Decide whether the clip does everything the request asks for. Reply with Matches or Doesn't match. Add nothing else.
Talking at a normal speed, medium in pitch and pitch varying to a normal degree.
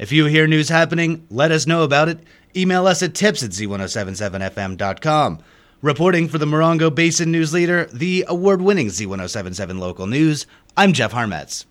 Doesn't match